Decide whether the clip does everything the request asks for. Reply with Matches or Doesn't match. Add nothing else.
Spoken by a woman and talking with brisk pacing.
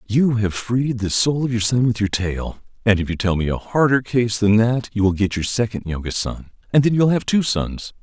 Doesn't match